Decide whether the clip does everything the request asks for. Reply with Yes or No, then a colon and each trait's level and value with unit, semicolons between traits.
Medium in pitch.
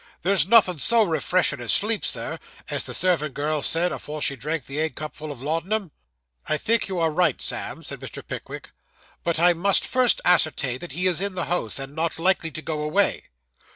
Yes: medium, 165 Hz